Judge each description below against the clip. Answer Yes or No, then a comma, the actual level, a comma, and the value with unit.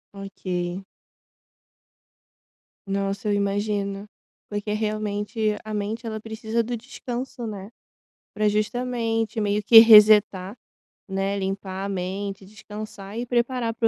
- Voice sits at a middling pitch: No, high, 210 Hz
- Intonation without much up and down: Yes, narrow, 2.2 semitones